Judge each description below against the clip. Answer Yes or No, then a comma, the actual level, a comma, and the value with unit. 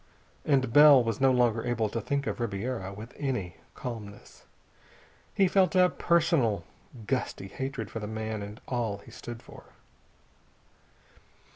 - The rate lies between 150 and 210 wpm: No, average, 140 wpm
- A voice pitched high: No, low, 120 Hz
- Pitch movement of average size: Yes, average, 4.1 semitones